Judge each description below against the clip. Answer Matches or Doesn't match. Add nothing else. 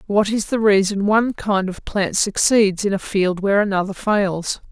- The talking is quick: Doesn't match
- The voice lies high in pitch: Matches